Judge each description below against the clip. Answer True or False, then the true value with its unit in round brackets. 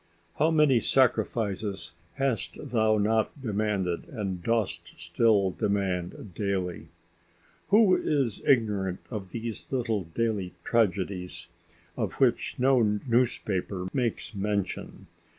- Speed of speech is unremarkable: False (100 wpm)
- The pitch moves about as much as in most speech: True (3.7 semitones)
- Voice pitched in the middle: False (105 Hz)